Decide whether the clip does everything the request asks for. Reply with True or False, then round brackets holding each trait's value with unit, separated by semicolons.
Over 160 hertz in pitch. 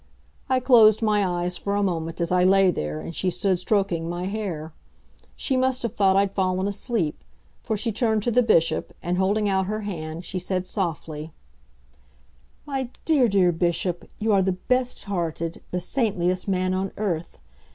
True (190 Hz)